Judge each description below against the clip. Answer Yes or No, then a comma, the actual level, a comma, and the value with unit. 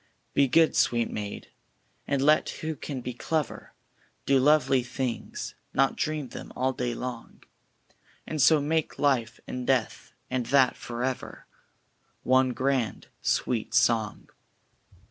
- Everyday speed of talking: No, slow, 130 wpm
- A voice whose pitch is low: Yes, low, 130 Hz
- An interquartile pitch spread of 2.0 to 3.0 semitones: Yes, narrow, 2.5 semitones